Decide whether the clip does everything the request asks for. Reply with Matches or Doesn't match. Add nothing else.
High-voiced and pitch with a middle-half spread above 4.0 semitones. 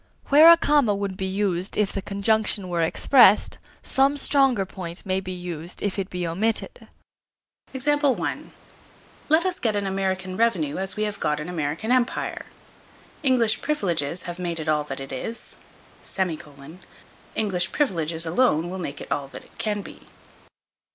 Matches